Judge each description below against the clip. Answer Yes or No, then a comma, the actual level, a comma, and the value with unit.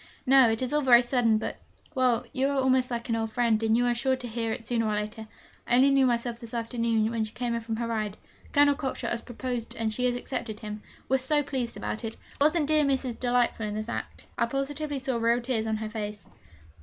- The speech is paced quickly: Yes, fast, 245 wpm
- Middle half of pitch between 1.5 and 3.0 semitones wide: Yes, narrow, 2.6 semitones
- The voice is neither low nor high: No, high, 240 Hz